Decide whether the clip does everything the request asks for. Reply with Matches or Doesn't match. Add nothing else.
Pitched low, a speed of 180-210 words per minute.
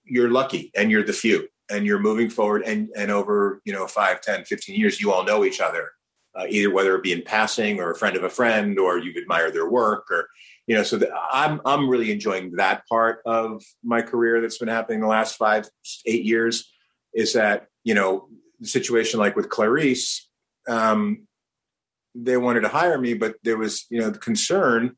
Matches